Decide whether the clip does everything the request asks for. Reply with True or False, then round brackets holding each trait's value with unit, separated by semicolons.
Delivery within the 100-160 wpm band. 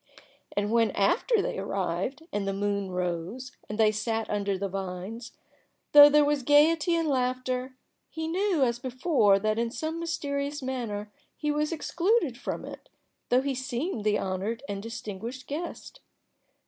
True (155 wpm)